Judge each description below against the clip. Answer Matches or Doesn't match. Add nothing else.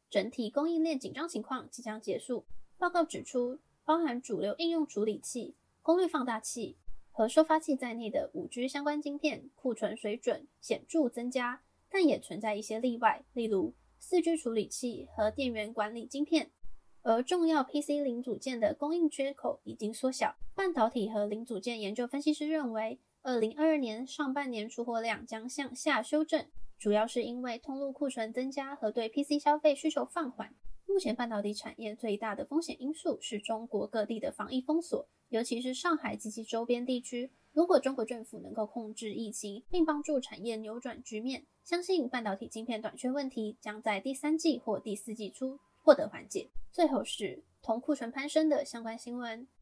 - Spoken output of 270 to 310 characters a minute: Matches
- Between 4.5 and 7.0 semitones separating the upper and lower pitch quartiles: Matches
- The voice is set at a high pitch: Matches